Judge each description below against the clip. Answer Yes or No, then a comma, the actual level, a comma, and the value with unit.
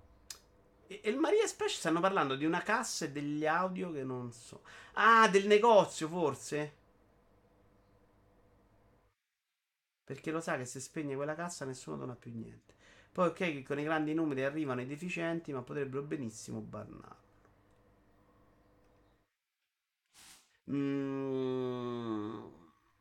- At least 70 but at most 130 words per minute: Yes, average, 120 wpm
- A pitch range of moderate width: No, wide, 8.1 semitones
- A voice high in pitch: No, low, 135 Hz